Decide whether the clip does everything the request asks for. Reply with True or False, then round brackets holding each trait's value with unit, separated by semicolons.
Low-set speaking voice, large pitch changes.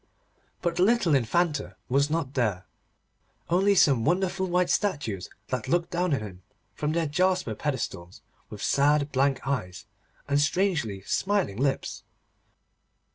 False (145 Hz; 6.2 semitones)